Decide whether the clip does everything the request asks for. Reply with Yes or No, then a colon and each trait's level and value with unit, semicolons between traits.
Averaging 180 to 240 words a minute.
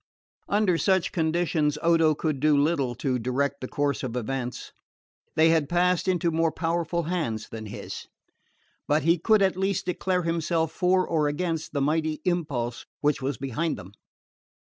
No: average, 160 wpm